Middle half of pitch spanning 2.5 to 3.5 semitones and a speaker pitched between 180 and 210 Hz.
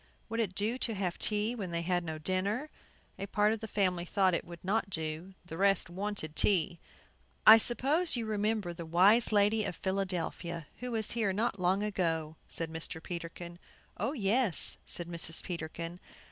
No: average, 3.9 semitones; high, 190 Hz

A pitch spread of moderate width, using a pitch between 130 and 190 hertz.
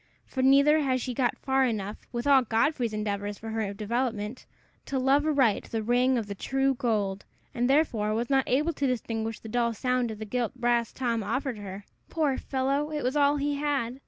No: average, 3.6 semitones; high, 245 Hz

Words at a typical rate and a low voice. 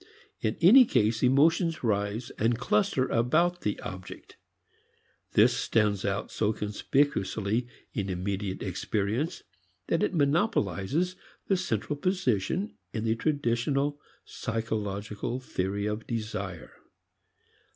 No: slow, 105 wpm; low, 115 Hz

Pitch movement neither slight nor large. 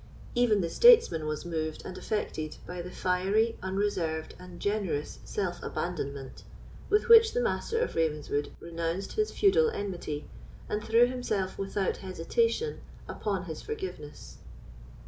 No: wide, 6.7 semitones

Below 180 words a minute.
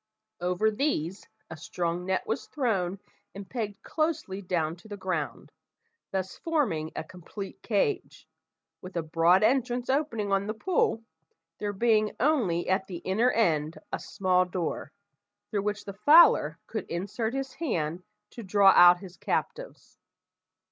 Yes: average, 145 wpm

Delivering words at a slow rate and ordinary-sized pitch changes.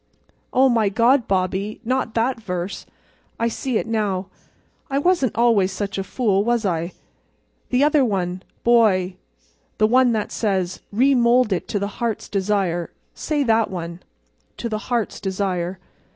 Yes: slow, 130 wpm; average, 4.1 semitones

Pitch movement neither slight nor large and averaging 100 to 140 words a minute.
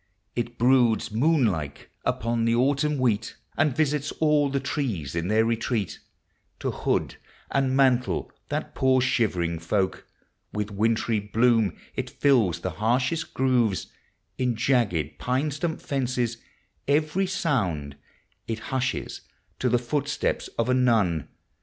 Yes: average, 4.2 semitones; slow, 135 wpm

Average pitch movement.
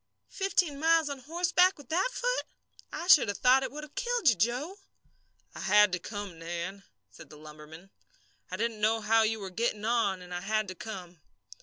No: wide, 8.0 semitones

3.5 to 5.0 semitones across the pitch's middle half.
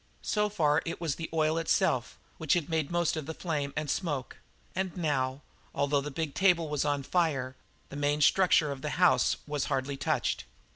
No: average, 2.9 semitones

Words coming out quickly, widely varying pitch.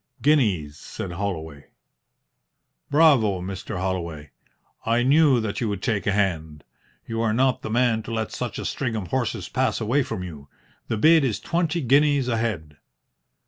No: average, 165 wpm; wide, 6.1 semitones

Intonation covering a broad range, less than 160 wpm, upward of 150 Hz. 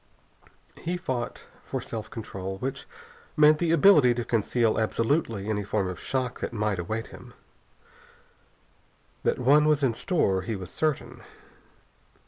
No: wide, 5.9 semitones; slow, 135 wpm; low, 115 Hz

